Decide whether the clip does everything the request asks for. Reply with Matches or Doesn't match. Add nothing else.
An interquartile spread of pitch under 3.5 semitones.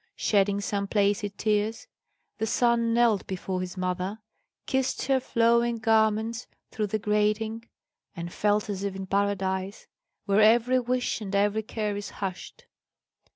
Matches